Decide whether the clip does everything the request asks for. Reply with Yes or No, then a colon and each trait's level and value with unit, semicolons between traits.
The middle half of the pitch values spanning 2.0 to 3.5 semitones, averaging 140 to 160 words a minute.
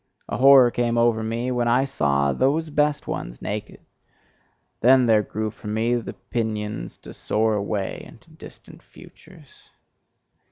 Yes: average, 3.0 semitones; average, 145 wpm